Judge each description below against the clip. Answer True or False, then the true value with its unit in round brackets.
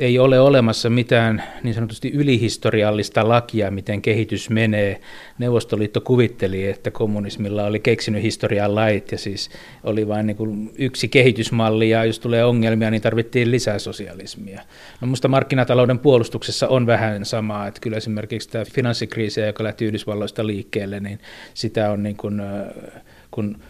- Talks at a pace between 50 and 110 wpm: False (140 wpm)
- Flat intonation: True (2.2 semitones)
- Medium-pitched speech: False (110 Hz)